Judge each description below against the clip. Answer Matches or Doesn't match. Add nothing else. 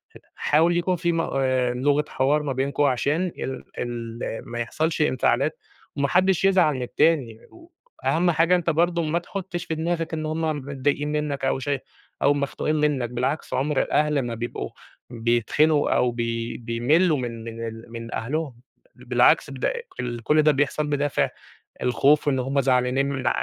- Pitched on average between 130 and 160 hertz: Matches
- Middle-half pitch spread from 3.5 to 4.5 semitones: Matches